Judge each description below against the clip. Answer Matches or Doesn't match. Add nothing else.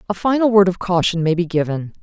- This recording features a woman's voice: Matches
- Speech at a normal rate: Doesn't match